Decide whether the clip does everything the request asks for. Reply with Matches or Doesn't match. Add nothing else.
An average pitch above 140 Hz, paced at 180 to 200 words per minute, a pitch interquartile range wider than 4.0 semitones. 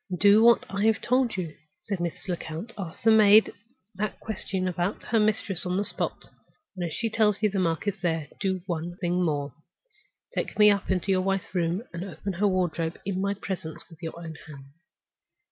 Doesn't match